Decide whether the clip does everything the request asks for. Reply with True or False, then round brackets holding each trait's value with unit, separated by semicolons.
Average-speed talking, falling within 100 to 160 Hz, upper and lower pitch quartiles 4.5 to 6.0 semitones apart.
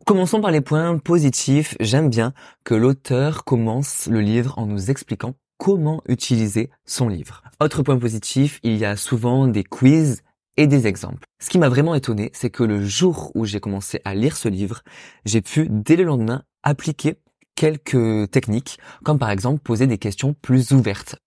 True (180 wpm; 130 Hz; 4.8 semitones)